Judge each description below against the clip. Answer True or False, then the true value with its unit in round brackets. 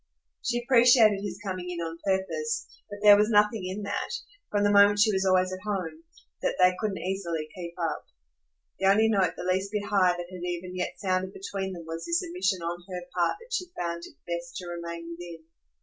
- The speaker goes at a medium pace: False (210 wpm)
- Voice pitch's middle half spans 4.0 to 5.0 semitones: False (2.9 semitones)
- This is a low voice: False (185 Hz)